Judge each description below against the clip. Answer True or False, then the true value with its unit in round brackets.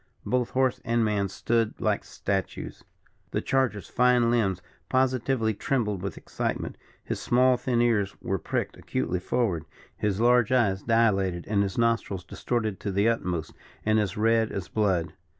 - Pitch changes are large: False (3.6 semitones)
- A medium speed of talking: True (150 wpm)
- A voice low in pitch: True (110 Hz)